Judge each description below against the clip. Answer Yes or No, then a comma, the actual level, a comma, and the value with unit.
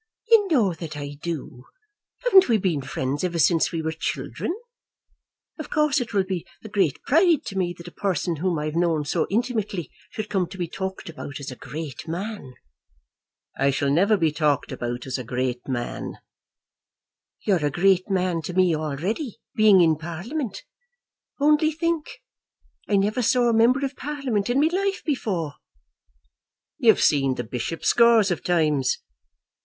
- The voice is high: No, medium, 180 Hz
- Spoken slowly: No, average, 170 wpm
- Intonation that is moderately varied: No, wide, 7.2 semitones